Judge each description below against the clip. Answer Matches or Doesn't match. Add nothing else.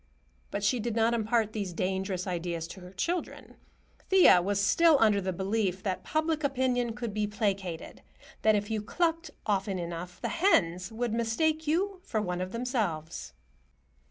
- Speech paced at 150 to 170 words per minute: Matches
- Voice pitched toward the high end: Matches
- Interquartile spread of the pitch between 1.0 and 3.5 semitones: Doesn't match